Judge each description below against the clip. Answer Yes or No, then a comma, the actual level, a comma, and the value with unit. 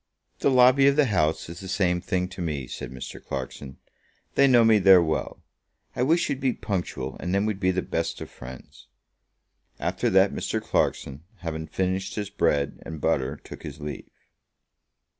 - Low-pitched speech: Yes, very low, 90 Hz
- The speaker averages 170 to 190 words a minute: Yes, average, 180 wpm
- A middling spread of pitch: No, wide, 5.7 semitones